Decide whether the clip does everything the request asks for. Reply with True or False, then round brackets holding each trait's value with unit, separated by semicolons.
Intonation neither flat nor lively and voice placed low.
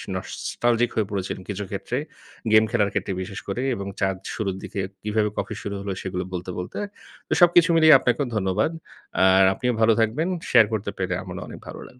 True (3.8 semitones; 105 Hz)